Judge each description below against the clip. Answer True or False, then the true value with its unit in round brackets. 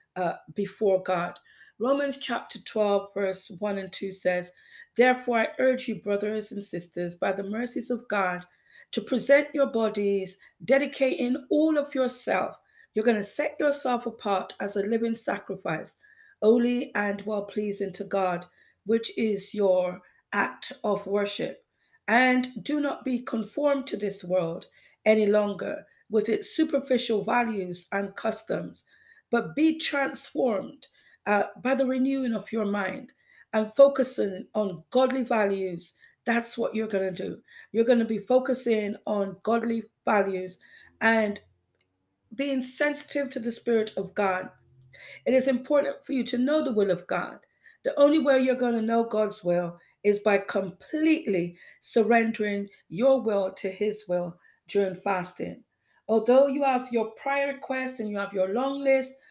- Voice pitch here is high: True (220 Hz)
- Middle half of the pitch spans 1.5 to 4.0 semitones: False (4.7 semitones)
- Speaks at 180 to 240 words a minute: False (150 wpm)